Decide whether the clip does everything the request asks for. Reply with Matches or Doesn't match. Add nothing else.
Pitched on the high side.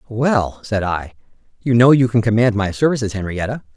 Doesn't match